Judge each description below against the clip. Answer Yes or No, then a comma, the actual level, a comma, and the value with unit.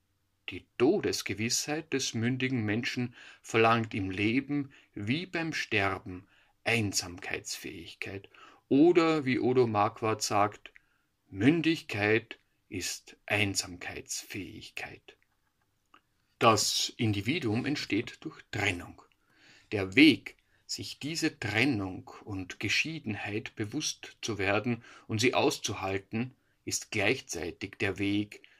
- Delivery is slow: Yes, slow, 90 wpm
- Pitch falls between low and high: No, low, 115 Hz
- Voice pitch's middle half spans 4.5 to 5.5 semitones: Yes, average, 4.9 semitones